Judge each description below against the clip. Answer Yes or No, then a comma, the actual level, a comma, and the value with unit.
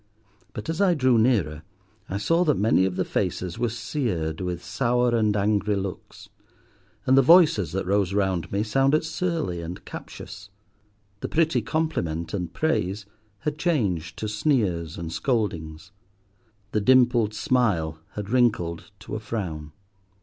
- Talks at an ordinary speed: Yes, average, 145 wpm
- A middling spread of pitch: No, wide, 6.3 semitones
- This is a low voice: Yes, low, 105 Hz